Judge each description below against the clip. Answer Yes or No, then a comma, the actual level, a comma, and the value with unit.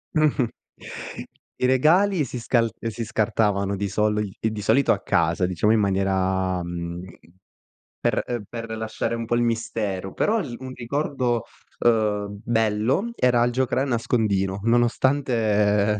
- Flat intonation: No, average, 3.2 semitones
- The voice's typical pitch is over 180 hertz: No, low, 115 Hz